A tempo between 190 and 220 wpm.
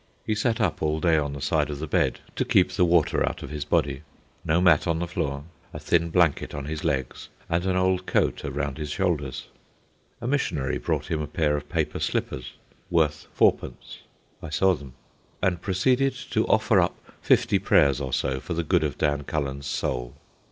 Yes: average, 195 wpm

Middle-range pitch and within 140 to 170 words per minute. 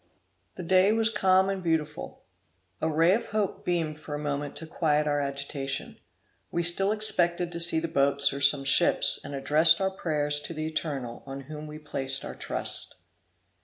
No: medium, 155 Hz; average, 180 wpm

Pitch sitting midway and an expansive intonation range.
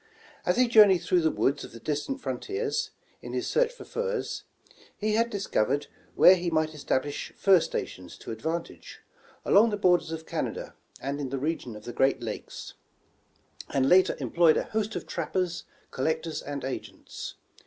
Yes: medium, 170 Hz; wide, 6.7 semitones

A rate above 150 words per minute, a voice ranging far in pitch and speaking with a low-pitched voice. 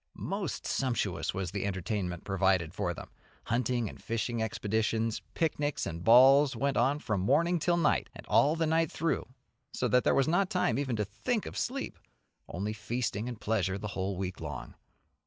Yes: average, 175 wpm; wide, 6.6 semitones; low, 115 Hz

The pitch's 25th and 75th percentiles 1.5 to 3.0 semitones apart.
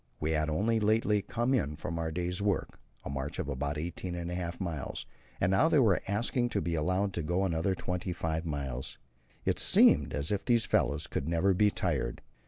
No: average, 4.6 semitones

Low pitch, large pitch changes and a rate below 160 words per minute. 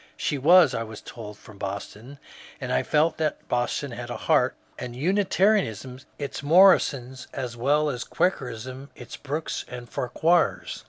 No: low, 130 Hz; average, 4.4 semitones; average, 150 wpm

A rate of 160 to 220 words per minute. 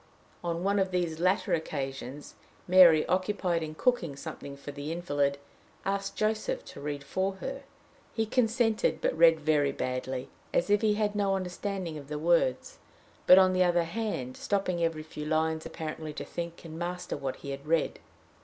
Yes: average, 170 wpm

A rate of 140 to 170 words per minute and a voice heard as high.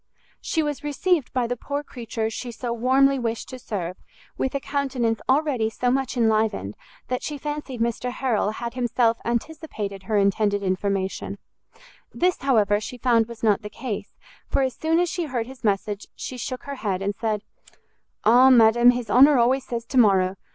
No: average, 180 wpm; high, 240 Hz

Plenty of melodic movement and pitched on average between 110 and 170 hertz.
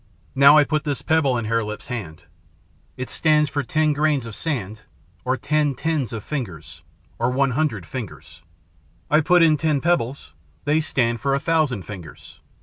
No: average, 4.9 semitones; medium, 140 Hz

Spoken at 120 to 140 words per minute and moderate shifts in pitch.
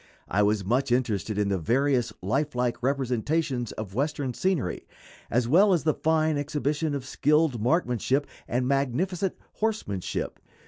Yes: slow, 135 wpm; average, 4.5 semitones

